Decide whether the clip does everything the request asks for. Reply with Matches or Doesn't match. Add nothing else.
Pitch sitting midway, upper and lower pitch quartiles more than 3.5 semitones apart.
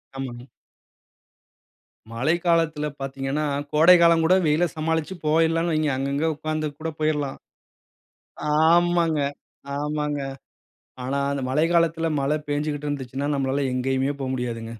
Doesn't match